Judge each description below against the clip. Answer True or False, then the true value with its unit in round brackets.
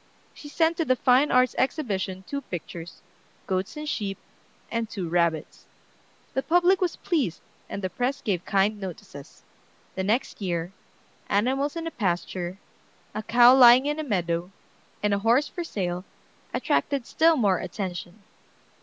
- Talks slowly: False (150 wpm)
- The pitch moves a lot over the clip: True (7.0 semitones)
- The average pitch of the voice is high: True (215 Hz)